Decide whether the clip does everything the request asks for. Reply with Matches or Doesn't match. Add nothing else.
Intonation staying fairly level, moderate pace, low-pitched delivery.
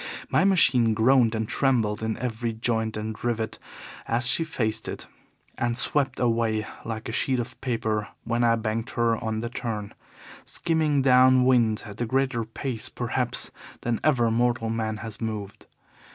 Matches